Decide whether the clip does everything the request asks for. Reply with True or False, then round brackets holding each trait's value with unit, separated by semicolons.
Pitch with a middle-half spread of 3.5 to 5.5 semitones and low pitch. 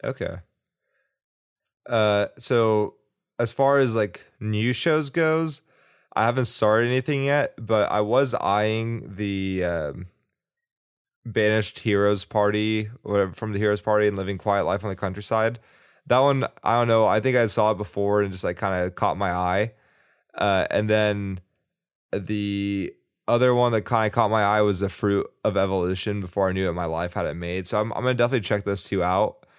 False (2.7 semitones; 105 Hz)